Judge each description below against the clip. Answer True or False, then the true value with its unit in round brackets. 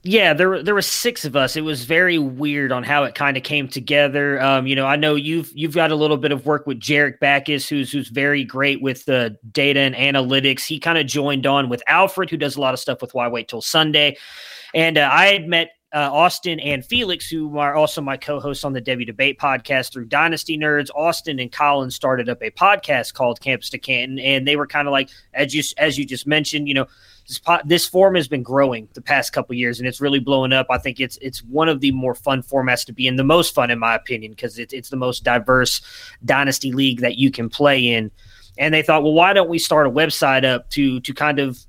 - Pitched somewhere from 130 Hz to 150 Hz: True (140 Hz)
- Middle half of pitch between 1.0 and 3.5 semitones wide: True (2.9 semitones)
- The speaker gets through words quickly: True (250 wpm)